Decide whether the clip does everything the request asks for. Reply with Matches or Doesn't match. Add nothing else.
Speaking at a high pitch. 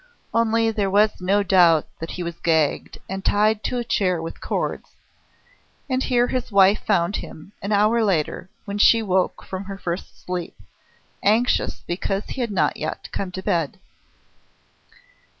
Matches